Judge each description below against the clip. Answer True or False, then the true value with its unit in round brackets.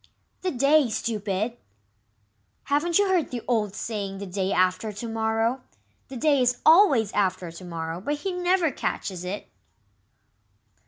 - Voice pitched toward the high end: True (225 Hz)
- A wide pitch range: True (6.8 semitones)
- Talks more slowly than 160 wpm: True (145 wpm)